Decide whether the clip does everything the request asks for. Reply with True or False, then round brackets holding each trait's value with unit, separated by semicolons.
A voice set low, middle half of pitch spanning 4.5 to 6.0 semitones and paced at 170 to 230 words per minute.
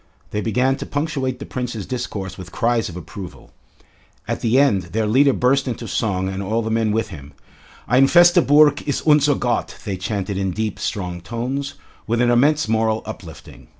True (115 Hz; 5.3 semitones; 185 wpm)